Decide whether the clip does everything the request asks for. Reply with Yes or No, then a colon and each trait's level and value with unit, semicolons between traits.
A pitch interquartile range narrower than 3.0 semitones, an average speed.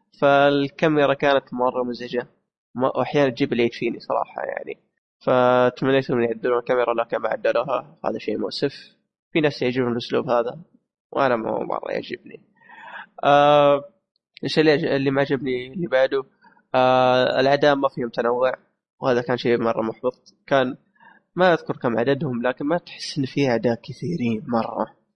No: narrow, 2.4 semitones; fast, 140 wpm